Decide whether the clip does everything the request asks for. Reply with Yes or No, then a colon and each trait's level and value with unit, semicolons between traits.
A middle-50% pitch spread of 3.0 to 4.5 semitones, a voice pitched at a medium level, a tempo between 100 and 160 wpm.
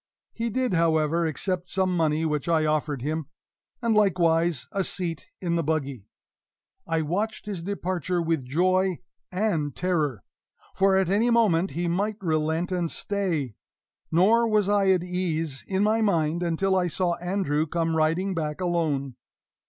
Yes: average, 3.3 semitones; medium, 175 Hz; average, 150 wpm